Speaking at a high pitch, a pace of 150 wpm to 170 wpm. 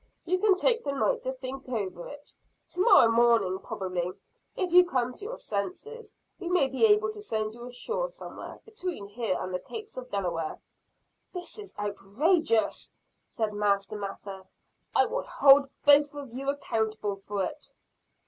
Yes: very high, 255 Hz; average, 165 wpm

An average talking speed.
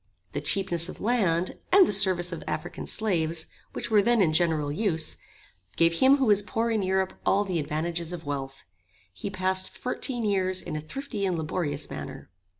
Yes: average, 180 wpm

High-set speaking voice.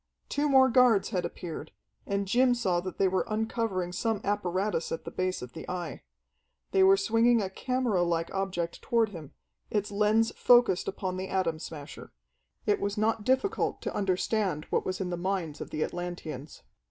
Yes: high, 195 Hz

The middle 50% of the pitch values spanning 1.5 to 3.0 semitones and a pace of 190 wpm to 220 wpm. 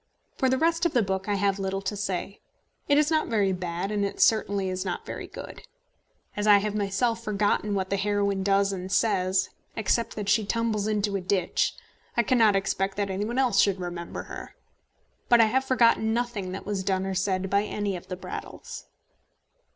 Yes: narrow, 2.4 semitones; average, 200 wpm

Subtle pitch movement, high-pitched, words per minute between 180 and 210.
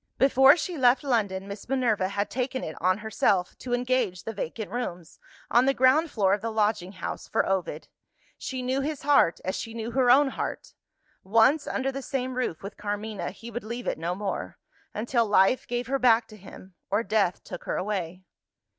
No: average, 4.6 semitones; high, 225 Hz; average, 195 wpm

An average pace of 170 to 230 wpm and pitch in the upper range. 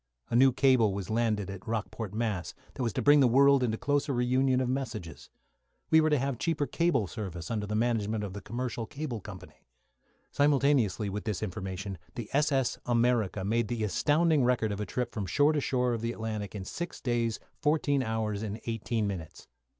No: average, 190 wpm; low, 115 Hz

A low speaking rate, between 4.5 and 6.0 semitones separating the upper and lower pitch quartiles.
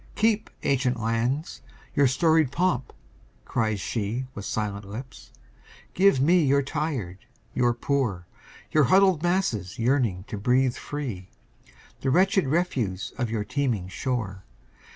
Yes: slow, 125 wpm; wide, 5.5 semitones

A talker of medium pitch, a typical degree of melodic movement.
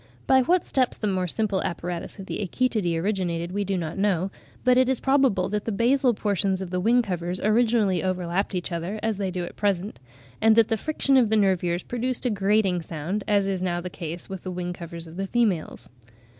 No: high, 195 Hz; average, 3.9 semitones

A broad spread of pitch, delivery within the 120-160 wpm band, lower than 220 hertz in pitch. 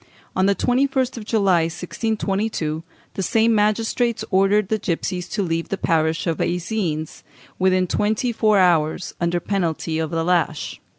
No: average, 4.4 semitones; average, 145 wpm; high, 190 Hz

